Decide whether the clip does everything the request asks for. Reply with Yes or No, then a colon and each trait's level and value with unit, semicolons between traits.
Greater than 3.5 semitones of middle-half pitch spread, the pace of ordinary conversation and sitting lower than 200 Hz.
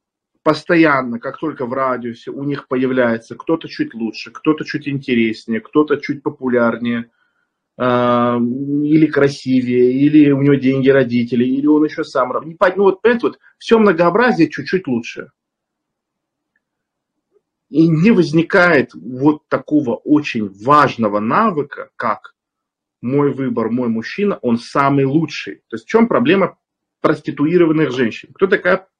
Yes: average, 4.6 semitones; average, 130 wpm; medium, 140 Hz